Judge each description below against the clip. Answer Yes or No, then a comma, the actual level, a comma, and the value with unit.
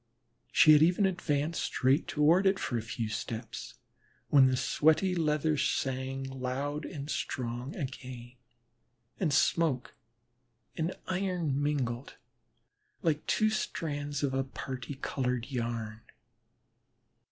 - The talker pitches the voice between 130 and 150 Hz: Yes, medium, 140 Hz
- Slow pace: Yes, slow, 115 wpm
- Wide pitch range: No, average, 3.7 semitones